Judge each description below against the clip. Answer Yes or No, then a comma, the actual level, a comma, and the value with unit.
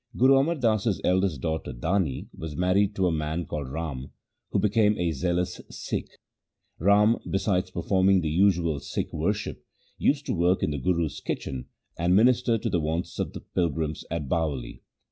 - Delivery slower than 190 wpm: Yes, average, 170 wpm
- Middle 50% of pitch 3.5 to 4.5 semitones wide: Yes, average, 4.2 semitones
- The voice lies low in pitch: Yes, very low, 90 Hz